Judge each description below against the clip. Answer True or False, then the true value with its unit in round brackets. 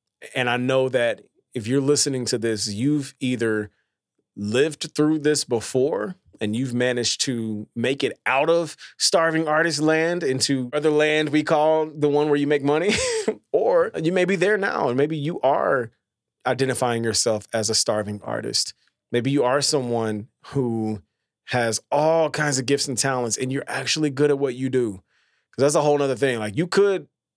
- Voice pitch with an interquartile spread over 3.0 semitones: True (4.1 semitones)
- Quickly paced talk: False (180 wpm)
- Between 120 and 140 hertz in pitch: True (135 Hz)